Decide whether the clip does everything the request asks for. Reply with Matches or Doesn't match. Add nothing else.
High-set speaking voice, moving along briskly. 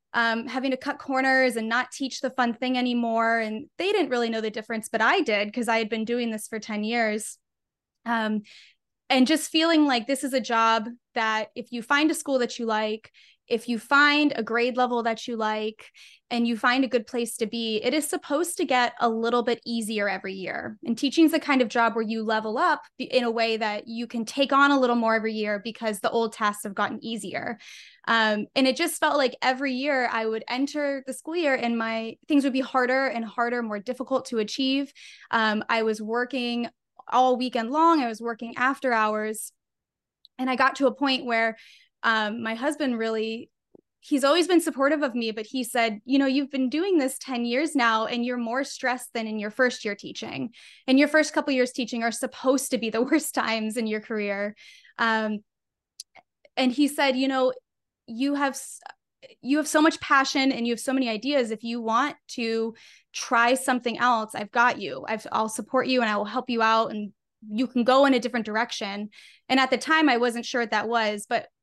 Matches